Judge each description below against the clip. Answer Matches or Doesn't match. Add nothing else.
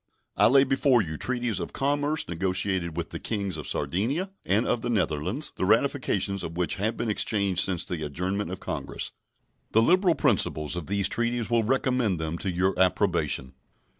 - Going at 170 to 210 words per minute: Matches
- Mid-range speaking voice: Doesn't match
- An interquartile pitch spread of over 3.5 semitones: Matches